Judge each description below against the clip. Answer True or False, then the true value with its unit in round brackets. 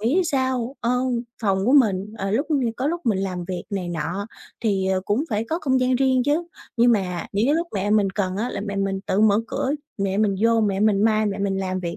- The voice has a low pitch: False (205 Hz)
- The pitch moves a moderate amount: True (4.2 semitones)